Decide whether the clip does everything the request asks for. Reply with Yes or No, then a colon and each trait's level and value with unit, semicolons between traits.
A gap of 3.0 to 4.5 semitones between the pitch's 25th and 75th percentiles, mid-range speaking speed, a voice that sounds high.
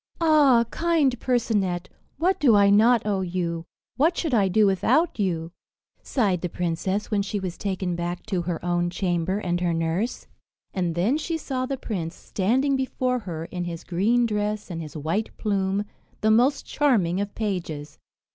No: wide, 5.6 semitones; average, 170 wpm; high, 200 Hz